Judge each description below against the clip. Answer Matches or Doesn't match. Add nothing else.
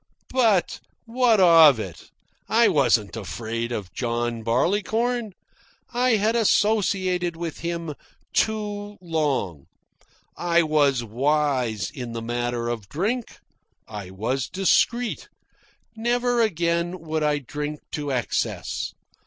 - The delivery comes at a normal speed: Doesn't match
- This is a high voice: Doesn't match